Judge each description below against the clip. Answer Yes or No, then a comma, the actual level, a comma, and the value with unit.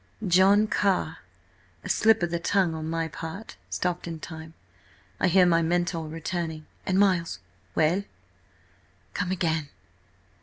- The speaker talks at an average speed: No, slow, 115 wpm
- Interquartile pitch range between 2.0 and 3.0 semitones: Yes, average, 2.7 semitones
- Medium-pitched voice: Yes, medium, 170 Hz